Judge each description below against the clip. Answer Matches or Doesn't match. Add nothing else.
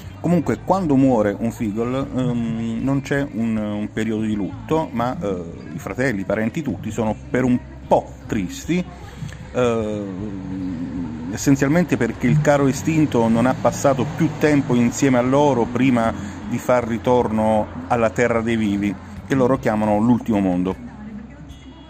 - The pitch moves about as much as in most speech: Matches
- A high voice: Doesn't match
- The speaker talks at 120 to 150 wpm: Matches